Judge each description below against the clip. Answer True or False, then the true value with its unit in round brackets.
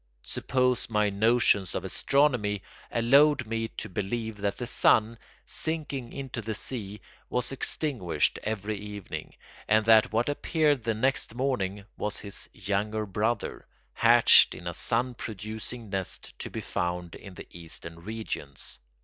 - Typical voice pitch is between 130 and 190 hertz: False (110 Hz)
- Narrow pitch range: False (3.5 semitones)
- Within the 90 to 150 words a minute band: True (140 wpm)